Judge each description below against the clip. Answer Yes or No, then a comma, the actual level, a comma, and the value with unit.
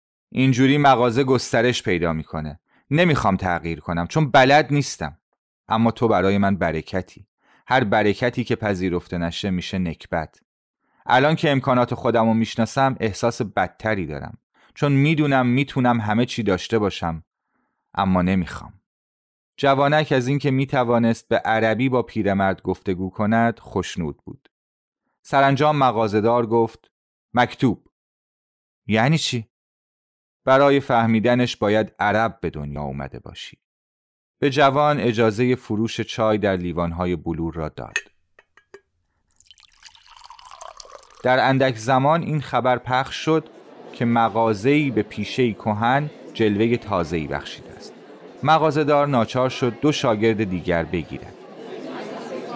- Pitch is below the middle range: Yes, low, 115 Hz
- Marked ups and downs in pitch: Yes, wide, 5.7 semitones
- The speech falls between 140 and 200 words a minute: No, average, 115 wpm